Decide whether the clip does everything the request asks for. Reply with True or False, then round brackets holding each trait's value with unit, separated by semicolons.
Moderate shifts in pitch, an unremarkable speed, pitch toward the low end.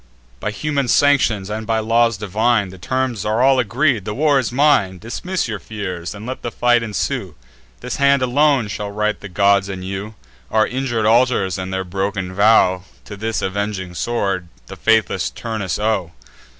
True (3.8 semitones; 175 wpm; 110 Hz)